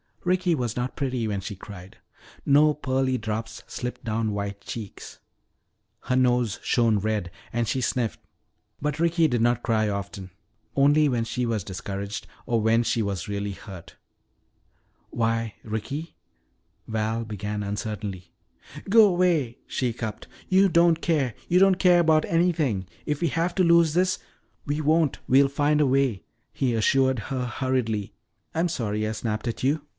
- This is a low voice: Yes, low, 120 Hz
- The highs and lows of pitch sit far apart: Yes, wide, 5.8 semitones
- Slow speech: No, average, 160 wpm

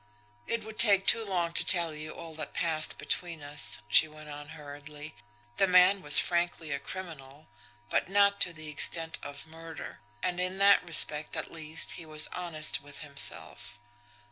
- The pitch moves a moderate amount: Yes, average, 3.2 semitones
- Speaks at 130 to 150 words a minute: No, average, 170 wpm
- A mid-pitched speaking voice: Yes, medium, 160 Hz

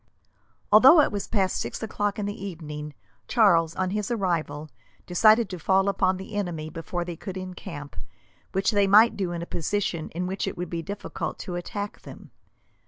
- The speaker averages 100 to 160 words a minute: No, average, 180 wpm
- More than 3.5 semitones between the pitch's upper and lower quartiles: No, average, 3.2 semitones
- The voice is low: No, high, 190 Hz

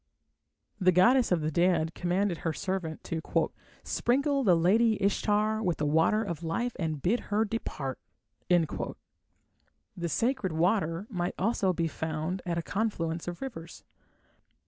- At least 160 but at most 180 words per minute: No, average, 140 wpm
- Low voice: No, medium, 180 Hz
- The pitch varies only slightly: No, average, 4.6 semitones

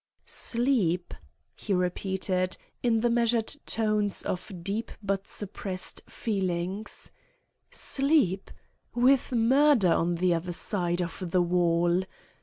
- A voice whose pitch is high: Yes, high, 195 Hz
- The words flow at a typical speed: No, slow, 105 wpm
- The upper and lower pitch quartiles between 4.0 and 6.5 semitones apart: Yes, average, 4.4 semitones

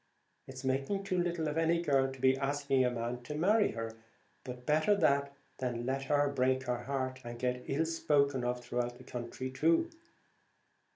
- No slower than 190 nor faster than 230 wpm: No, average, 180 wpm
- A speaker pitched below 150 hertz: Yes, low, 135 Hz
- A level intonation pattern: No, average, 3.2 semitones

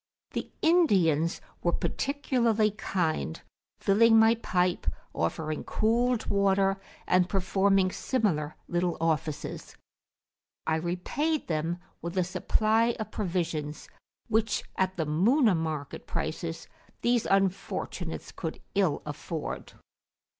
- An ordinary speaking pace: No, slow, 105 wpm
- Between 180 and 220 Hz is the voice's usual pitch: Yes, high, 190 Hz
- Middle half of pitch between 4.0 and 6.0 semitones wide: Yes, average, 5.2 semitones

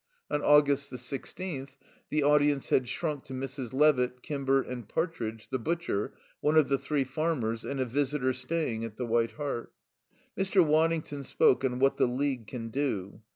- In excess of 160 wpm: Yes, average, 170 wpm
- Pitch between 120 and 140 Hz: Yes, low, 135 Hz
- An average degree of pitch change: Yes, average, 3.1 semitones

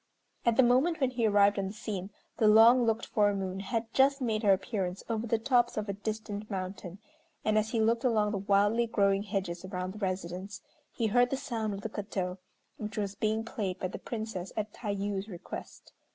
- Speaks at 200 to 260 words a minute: Yes, fast, 205 wpm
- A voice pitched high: Yes, high, 210 Hz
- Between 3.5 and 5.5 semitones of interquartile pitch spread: No, narrow, 2.6 semitones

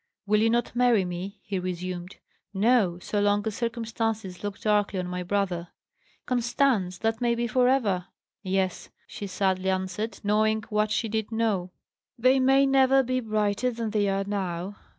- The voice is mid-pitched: No, high, 210 Hz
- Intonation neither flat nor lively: Yes, average, 3.5 semitones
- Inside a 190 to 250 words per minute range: No, average, 165 wpm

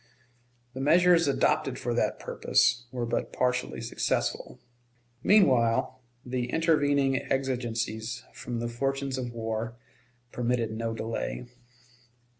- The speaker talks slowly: Yes, slow, 105 wpm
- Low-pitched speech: Yes, low, 125 Hz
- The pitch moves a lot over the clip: No, average, 2.9 semitones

